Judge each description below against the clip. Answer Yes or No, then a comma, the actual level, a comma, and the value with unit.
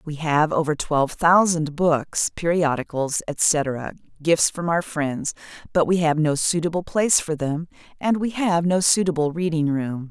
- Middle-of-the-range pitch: Yes, medium, 160 Hz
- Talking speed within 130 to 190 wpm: Yes, average, 160 wpm